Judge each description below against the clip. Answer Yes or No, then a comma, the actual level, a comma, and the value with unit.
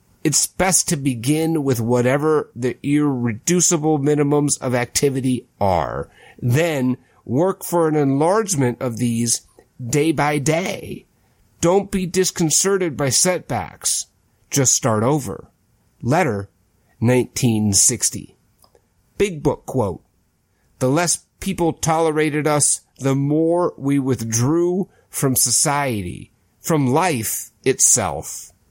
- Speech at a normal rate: No, slow, 100 wpm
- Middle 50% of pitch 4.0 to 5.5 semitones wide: Yes, average, 4.9 semitones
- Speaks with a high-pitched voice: No, medium, 140 Hz